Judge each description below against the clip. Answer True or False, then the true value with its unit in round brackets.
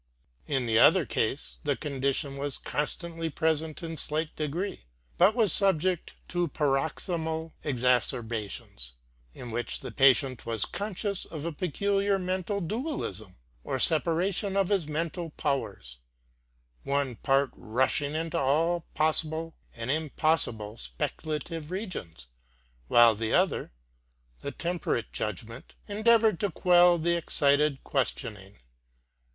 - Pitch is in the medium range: True (155 Hz)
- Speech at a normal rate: False (120 wpm)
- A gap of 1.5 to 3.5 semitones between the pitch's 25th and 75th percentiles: False (5.0 semitones)